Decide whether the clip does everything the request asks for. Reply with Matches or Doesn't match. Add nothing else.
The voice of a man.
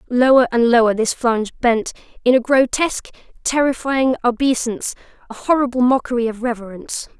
Doesn't match